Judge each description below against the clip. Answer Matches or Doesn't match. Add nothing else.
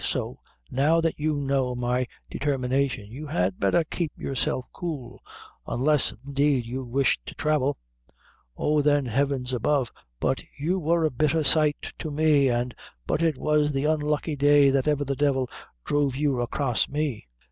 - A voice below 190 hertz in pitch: Matches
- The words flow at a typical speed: Matches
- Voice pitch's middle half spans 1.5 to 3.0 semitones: Matches